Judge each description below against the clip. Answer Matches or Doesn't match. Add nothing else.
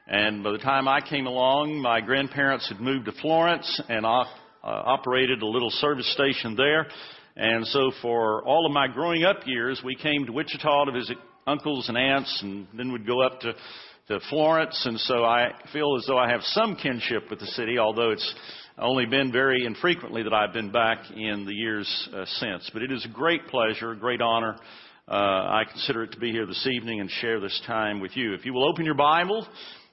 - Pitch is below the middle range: Matches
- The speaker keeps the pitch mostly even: Doesn't match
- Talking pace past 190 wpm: Matches